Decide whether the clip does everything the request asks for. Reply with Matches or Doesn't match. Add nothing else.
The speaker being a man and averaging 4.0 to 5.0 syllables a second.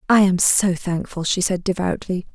Doesn't match